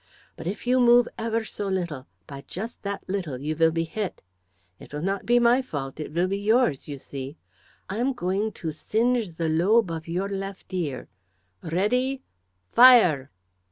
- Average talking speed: Yes, average, 175 wpm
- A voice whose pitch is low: No, high, 190 Hz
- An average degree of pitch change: No, wide, 6.2 semitones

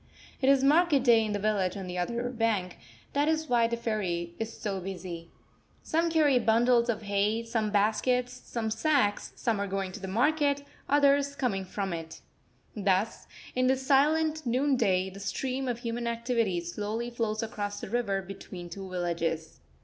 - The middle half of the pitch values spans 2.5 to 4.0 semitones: No, average, 4.7 semitones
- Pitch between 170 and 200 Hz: No, high, 225 Hz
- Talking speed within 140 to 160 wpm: No, average, 170 wpm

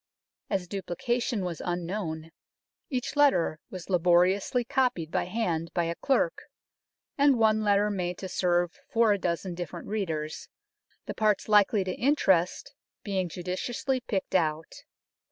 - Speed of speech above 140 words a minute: No, slow, 135 wpm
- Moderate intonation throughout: Yes, average, 4.1 semitones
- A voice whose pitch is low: No, high, 190 Hz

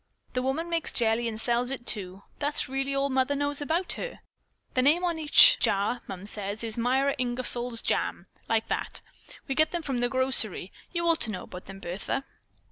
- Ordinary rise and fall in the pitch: Yes, average, 4.4 semitones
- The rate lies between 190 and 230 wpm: Yes, average, 195 wpm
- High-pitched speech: Yes, very high, 255 Hz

